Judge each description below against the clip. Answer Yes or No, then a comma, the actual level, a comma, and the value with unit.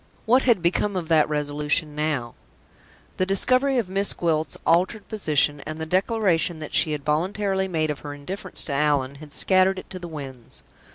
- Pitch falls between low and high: Yes, medium, 165 Hz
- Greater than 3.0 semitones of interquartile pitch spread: Yes, average, 4.3 semitones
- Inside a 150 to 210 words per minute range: Yes, average, 180 wpm